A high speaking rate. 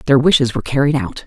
Yes: fast, 235 wpm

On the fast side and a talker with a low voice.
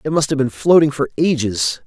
No: fast, 225 wpm; medium, 145 Hz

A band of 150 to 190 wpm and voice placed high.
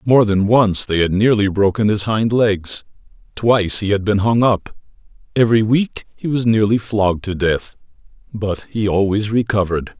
No: average, 170 wpm; low, 105 Hz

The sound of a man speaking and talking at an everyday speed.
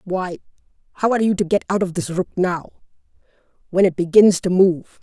No: female; average, 190 wpm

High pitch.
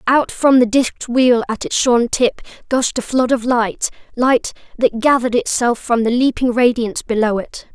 Yes: high, 240 Hz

